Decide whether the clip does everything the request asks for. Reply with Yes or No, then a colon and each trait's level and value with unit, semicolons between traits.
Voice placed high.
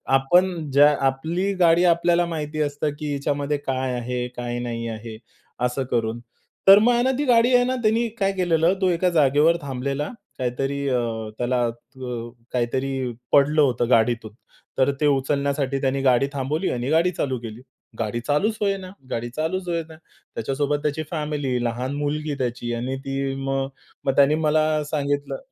No: medium, 140 Hz